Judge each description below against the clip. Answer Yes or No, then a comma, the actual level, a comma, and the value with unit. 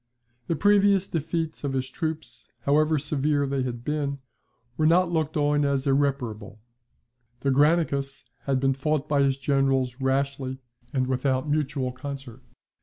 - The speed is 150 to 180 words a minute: No, average, 140 wpm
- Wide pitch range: No, narrow, 2.4 semitones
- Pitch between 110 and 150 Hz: Yes, medium, 140 Hz